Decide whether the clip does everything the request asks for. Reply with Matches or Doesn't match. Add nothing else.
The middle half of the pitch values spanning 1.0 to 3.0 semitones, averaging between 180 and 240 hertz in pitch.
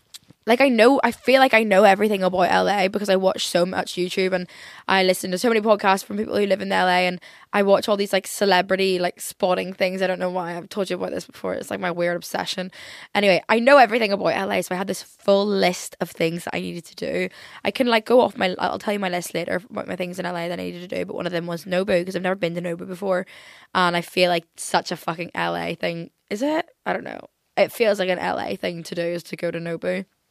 Matches